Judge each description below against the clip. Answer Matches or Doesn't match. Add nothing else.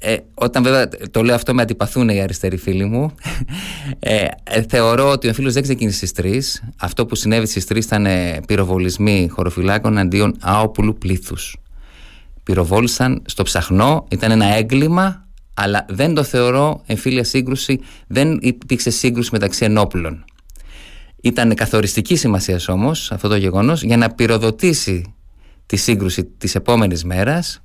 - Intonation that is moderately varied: Matches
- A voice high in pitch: Doesn't match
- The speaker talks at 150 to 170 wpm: Doesn't match